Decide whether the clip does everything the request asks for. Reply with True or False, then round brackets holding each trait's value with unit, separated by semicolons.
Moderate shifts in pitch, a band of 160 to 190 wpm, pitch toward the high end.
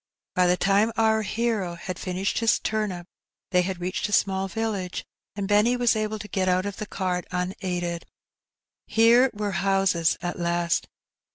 True (3.1 semitones; 165 wpm; 195 Hz)